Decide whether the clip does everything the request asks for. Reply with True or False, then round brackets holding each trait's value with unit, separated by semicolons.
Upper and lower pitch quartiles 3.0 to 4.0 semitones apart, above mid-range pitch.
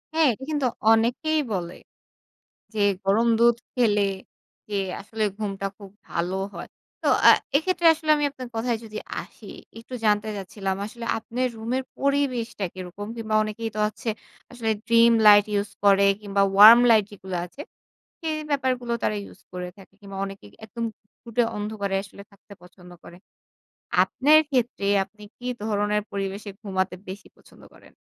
True (3.4 semitones; 215 Hz)